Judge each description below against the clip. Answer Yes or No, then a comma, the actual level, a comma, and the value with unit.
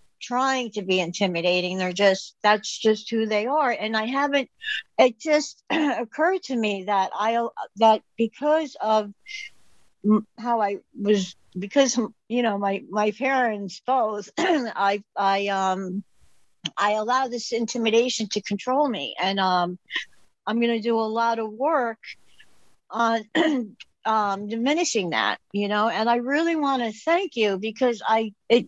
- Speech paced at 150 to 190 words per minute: No, average, 140 wpm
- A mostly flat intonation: No, average, 3.8 semitones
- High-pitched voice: Yes, high, 225 Hz